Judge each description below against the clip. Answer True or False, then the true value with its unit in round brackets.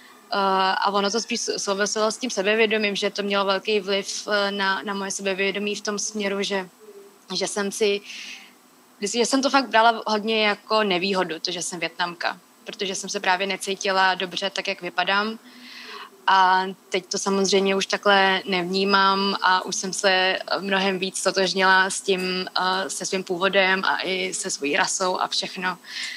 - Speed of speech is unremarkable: True (160 wpm)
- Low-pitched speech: False (195 Hz)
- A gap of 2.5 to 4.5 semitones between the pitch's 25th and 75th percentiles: False (1.4 semitones)